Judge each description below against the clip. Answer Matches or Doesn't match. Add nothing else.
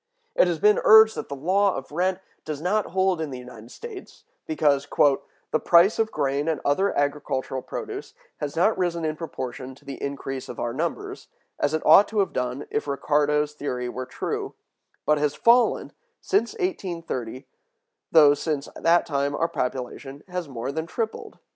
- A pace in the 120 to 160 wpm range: Doesn't match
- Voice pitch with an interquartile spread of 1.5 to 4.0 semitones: Doesn't match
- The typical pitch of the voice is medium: Matches